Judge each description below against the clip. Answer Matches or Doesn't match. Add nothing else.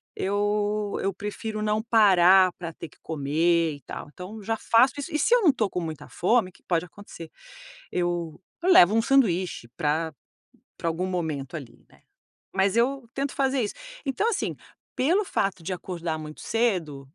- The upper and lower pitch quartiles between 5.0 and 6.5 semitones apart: Matches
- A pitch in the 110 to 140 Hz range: Doesn't match